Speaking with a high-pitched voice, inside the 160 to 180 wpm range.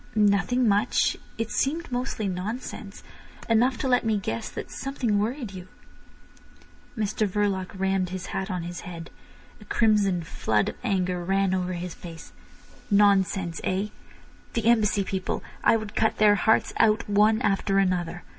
No: high, 200 Hz; average, 145 wpm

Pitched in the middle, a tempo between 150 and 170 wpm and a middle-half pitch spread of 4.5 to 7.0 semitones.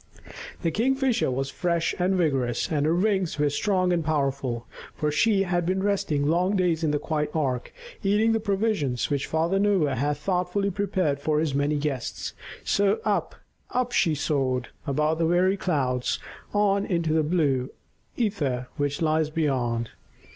Yes: medium, 160 Hz; average, 160 wpm; average, 5.1 semitones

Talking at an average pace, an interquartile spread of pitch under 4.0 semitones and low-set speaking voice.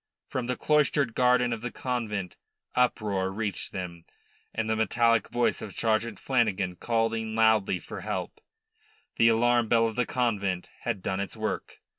Yes: average, 155 wpm; average, 2.9 semitones; low, 115 Hz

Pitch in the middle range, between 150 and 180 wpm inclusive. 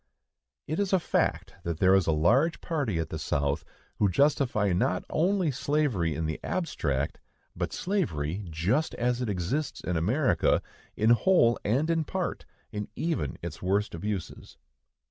No: low, 105 Hz; average, 155 wpm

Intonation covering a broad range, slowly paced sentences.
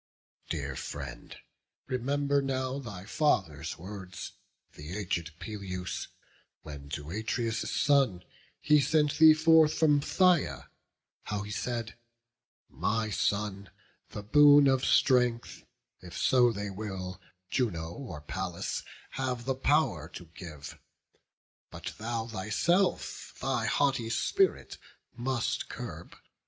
Yes: wide, 6.8 semitones; slow, 110 wpm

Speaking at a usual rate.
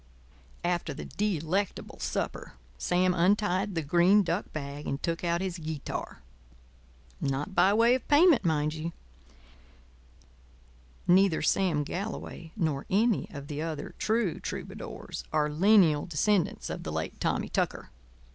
No: slow, 130 wpm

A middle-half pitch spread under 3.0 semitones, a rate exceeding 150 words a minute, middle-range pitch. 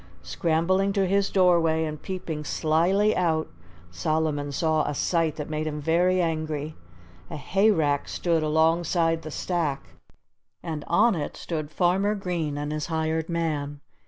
No: narrow, 2.5 semitones; average, 140 wpm; medium, 160 Hz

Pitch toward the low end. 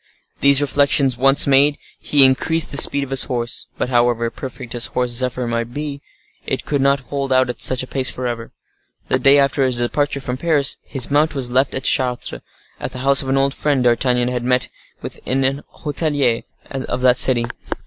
Yes: low, 130 Hz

